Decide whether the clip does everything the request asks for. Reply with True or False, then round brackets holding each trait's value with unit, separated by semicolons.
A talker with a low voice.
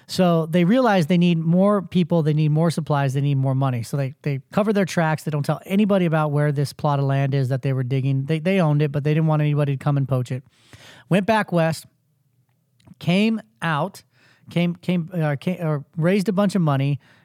False (155 Hz)